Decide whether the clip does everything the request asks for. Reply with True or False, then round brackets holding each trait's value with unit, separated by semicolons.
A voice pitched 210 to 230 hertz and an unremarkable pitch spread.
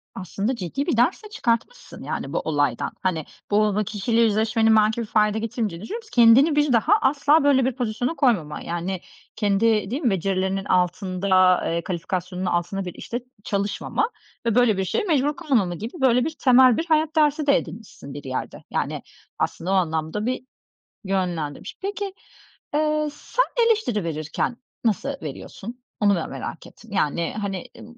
False (215 Hz; 6.0 semitones)